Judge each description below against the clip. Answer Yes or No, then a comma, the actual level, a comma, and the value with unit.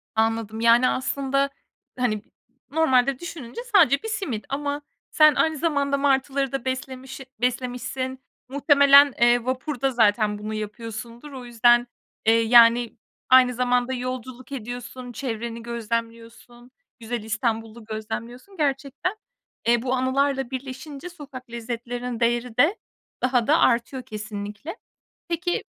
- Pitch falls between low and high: No, very high, 250 Hz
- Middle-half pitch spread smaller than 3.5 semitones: Yes, average, 2.9 semitones